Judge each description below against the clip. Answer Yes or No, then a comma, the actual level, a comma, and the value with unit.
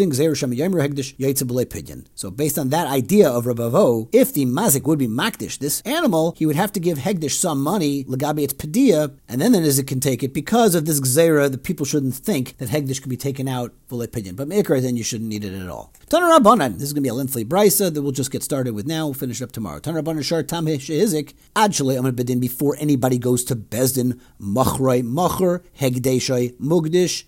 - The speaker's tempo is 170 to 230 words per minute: Yes, average, 200 wpm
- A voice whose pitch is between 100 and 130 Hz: No, medium, 140 Hz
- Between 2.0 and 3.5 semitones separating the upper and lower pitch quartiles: No, average, 4.0 semitones